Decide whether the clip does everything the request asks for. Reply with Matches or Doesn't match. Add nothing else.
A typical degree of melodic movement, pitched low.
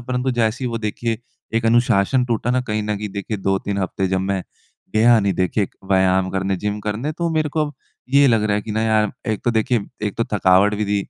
Matches